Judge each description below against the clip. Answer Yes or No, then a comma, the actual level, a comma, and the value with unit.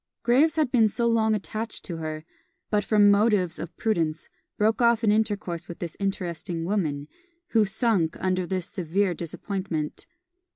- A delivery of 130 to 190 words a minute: Yes, average, 150 wpm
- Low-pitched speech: No, high, 195 Hz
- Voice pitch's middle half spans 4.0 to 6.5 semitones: Yes, average, 4.5 semitones